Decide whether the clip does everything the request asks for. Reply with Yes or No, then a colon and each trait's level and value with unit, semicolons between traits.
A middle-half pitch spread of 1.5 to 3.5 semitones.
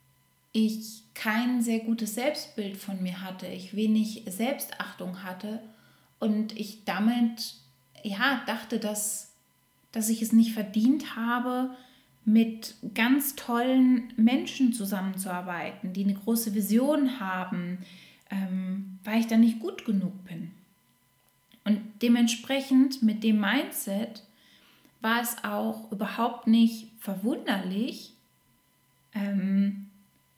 Yes: average, 2.9 semitones